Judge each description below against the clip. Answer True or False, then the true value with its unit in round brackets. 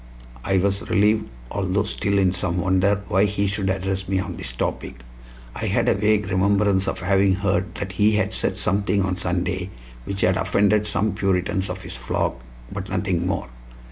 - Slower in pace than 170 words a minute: False (180 wpm)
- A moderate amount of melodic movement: False (1.6 semitones)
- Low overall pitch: True (95 Hz)